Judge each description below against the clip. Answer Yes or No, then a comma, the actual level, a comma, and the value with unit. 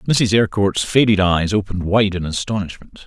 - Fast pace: No, average, 155 wpm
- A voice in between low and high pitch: No, low, 100 Hz